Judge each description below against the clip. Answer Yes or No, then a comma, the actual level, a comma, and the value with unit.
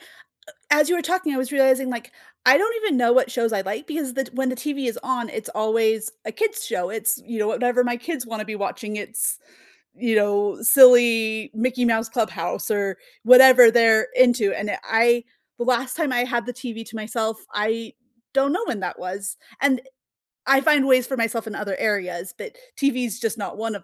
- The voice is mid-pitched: No, high, 235 Hz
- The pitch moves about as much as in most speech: Yes, average, 3.0 semitones